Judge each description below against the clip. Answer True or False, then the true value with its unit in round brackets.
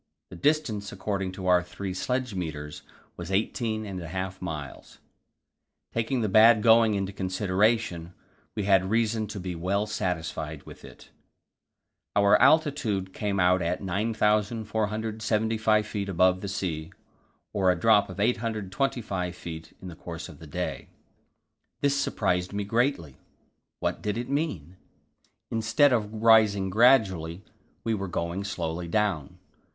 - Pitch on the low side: True (100 Hz)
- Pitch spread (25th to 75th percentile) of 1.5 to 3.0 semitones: False (3.5 semitones)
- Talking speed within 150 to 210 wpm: False (135 wpm)